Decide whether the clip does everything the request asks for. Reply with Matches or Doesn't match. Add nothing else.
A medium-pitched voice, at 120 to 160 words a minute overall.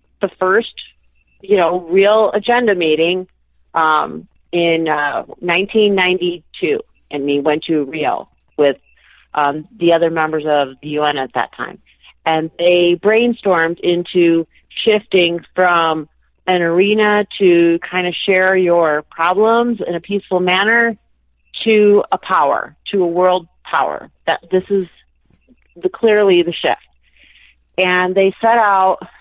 Matches